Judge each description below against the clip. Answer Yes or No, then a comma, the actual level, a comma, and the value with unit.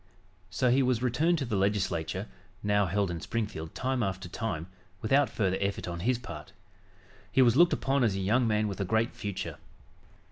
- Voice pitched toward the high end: No, low, 105 Hz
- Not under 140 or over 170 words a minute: No, average, 185 wpm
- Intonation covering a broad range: No, average, 4.6 semitones